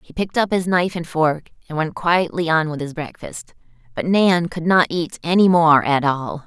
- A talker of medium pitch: Yes, medium, 165 Hz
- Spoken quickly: Yes, fast, 215 wpm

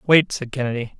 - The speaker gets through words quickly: No, average, 180 wpm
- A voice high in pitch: No, low, 130 Hz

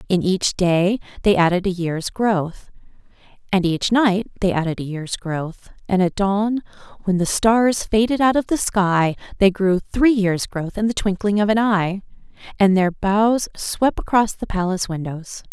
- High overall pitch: Yes, high, 195 Hz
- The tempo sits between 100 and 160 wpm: No, average, 180 wpm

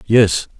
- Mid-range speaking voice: No, low, 100 Hz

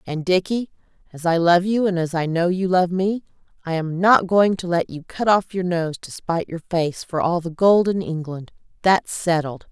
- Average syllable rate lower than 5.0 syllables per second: Yes, 4.8 syllables/s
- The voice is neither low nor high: Yes, medium, 175 Hz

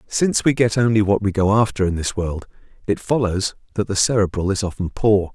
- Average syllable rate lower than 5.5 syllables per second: No, 5.7 syllables/s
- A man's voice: Yes, male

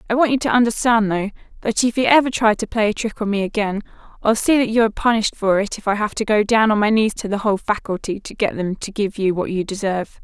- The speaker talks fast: Yes, fast, 280 wpm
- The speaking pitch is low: No, high, 215 Hz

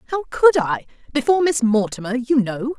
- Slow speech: No, average, 170 wpm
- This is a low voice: No, very high, 260 Hz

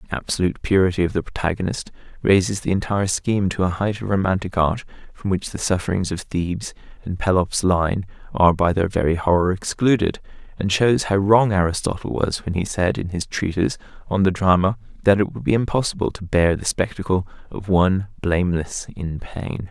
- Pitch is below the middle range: Yes, very low, 95 Hz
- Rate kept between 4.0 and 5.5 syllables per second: No, 5.7 syllables/s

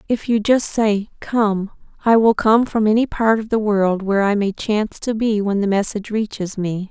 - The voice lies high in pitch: Yes, high, 210 Hz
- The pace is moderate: No, fast, 215 wpm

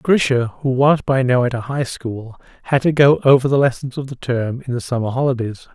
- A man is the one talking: Yes, male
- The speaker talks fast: Yes, fast, 230 wpm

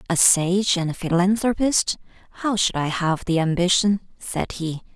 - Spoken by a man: No, female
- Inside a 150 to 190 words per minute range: Yes, average, 155 wpm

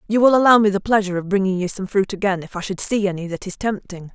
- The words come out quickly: Yes, fast, 290 wpm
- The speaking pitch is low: No, high, 195 Hz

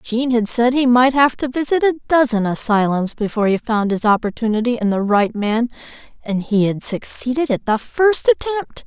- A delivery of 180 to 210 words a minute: Yes, average, 190 wpm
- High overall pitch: Yes, high, 240 Hz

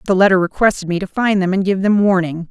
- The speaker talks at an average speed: No, fast, 265 wpm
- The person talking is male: No, female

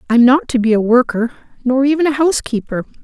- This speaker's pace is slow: No, average, 200 wpm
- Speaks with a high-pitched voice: Yes, very high, 255 Hz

